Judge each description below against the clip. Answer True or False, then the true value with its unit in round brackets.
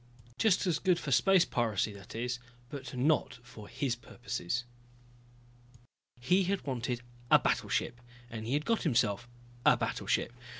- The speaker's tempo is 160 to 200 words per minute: False (140 wpm)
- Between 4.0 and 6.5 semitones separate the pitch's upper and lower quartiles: True (4.8 semitones)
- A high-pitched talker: False (125 Hz)